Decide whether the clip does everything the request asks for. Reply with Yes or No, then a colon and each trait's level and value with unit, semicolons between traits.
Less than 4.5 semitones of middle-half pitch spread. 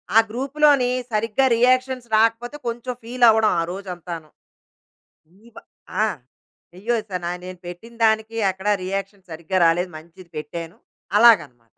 No: average, 5.1 semitones